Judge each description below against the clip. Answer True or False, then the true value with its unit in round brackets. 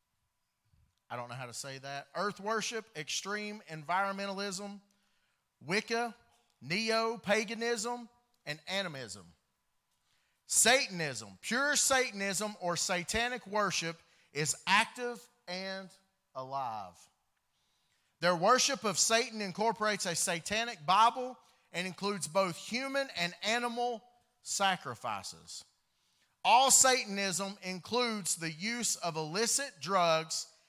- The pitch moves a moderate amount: False (6.1 semitones)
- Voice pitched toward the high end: True (195 Hz)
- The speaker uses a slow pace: True (95 wpm)